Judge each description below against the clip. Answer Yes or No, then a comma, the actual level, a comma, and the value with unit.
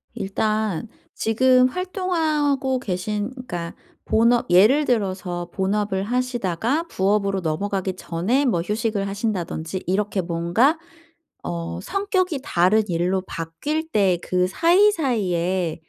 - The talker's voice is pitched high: Yes, high, 205 Hz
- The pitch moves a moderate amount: No, wide, 6.0 semitones